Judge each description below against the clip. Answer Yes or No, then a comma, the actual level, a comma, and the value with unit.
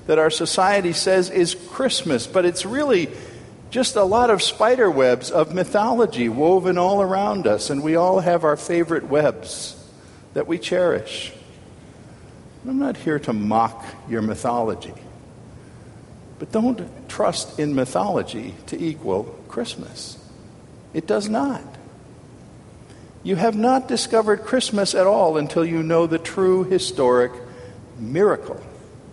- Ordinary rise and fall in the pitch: No, wide, 5.7 semitones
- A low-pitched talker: No, medium, 180 Hz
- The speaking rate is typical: No, slow, 130 wpm